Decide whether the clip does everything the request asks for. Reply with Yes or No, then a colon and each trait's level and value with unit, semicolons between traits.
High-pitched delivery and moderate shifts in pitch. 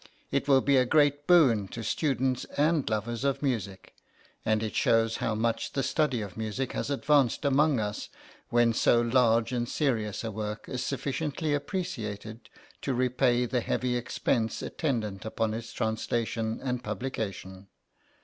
No: low, 120 Hz; average, 3.7 semitones